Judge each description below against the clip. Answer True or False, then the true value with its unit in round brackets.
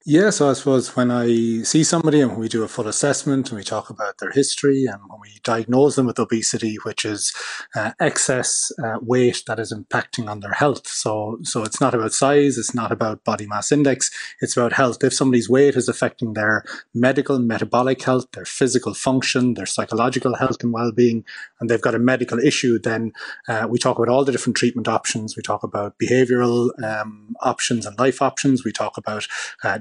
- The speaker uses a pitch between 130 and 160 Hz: False (120 Hz)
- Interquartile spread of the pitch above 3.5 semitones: False (2.7 semitones)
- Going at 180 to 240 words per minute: True (200 wpm)